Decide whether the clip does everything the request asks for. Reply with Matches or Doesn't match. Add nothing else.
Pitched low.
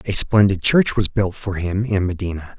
Matches